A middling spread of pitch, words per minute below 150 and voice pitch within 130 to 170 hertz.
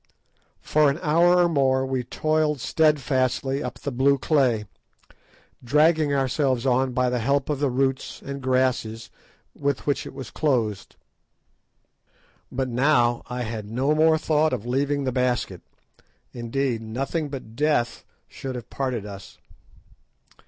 Yes: average, 3.0 semitones; average, 140 wpm; low, 135 Hz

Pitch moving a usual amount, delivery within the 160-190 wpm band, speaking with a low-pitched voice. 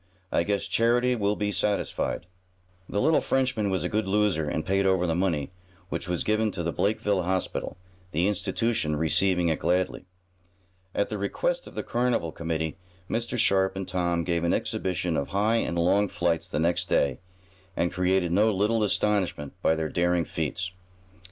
Yes: average, 3.5 semitones; average, 170 wpm; very low, 95 Hz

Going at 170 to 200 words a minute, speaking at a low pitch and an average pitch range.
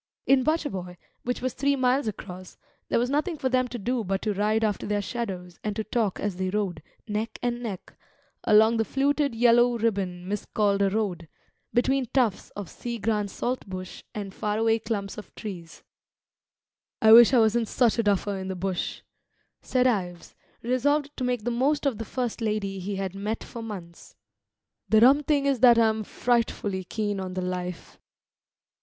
No: average, 180 wpm; high, 220 Hz; average, 3.9 semitones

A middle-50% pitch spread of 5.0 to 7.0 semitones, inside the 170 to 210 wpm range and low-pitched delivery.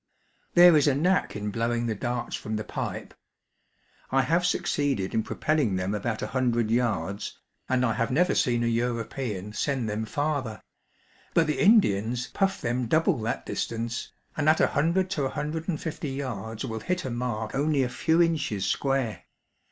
Yes: average, 5.3 semitones; average, 175 wpm; low, 125 Hz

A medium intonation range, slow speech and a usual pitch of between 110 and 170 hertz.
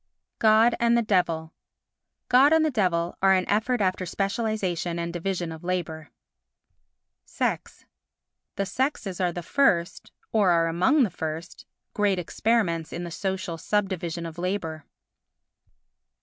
No: average, 4.2 semitones; slow, 130 wpm; medium, 185 Hz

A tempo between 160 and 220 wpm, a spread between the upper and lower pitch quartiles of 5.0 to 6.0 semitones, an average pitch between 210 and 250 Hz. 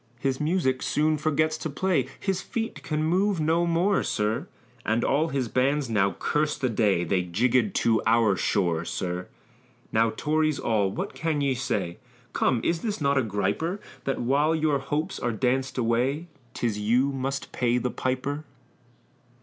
No: average, 165 wpm; wide, 5.4 semitones; low, 130 Hz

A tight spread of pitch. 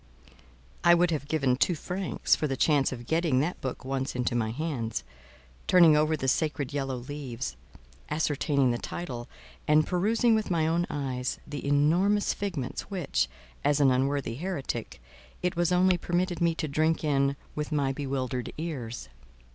No: average, 4.3 semitones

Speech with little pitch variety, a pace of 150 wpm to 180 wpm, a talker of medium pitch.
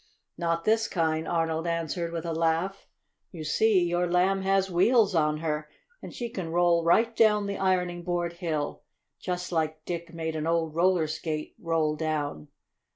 Yes: narrow, 2.3 semitones; average, 165 wpm; medium, 170 Hz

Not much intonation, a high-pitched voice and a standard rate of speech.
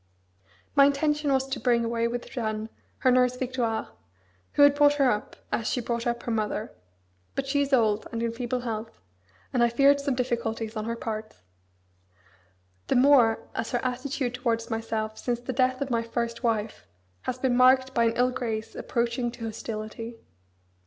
Yes: narrow, 2.2 semitones; high, 240 Hz; average, 180 wpm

